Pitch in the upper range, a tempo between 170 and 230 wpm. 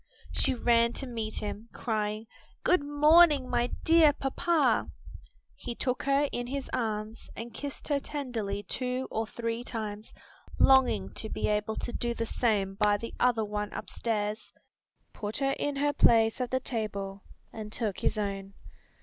No: high, 230 Hz; average, 160 wpm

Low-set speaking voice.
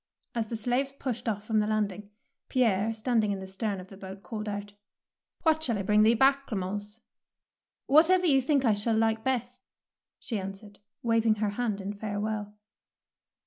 No: high, 215 Hz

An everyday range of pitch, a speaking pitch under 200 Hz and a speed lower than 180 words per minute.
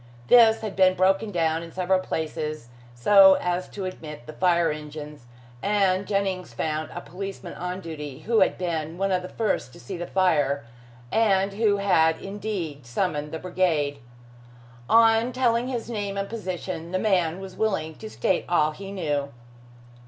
Yes: average, 3.9 semitones; medium, 185 Hz; average, 165 wpm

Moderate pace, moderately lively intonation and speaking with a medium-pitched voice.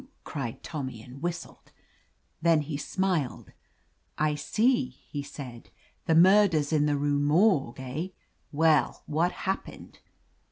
No: slow, 125 wpm; average, 3.3 semitones; medium, 150 Hz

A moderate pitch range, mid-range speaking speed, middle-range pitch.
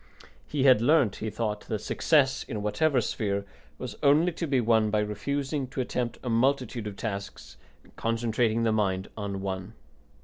No: average, 4.2 semitones; average, 170 wpm; low, 115 Hz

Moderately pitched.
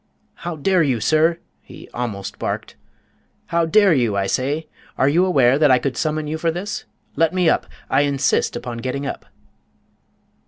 Yes: medium, 150 Hz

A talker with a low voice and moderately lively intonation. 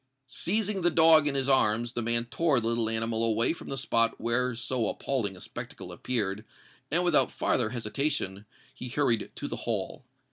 Yes: low, 120 Hz; average, 4.3 semitones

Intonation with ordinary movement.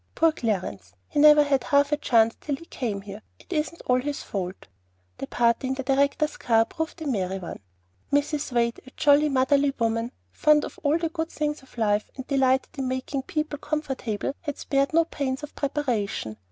Yes: average, 4.3 semitones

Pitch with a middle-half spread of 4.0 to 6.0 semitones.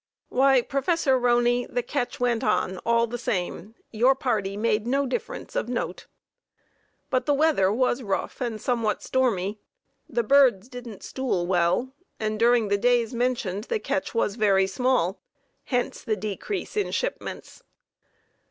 No: average, 3.6 semitones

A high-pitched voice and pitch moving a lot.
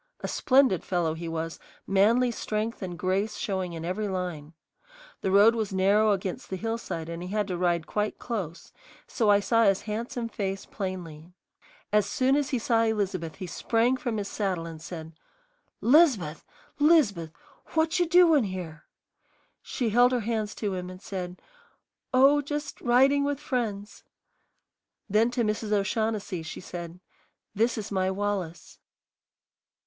No: high, 205 Hz; average, 4.3 semitones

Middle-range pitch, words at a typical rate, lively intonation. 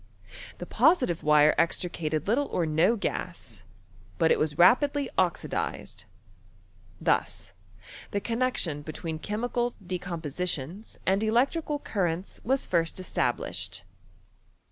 No: medium, 180 Hz; slow, 105 wpm; wide, 6.8 semitones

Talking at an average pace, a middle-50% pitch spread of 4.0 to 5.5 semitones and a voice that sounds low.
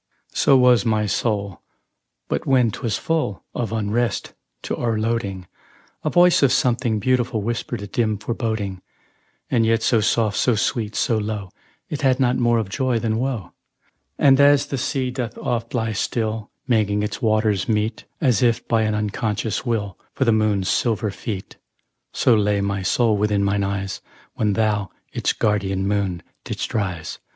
No: average, 160 wpm; average, 2.7 semitones; low, 110 Hz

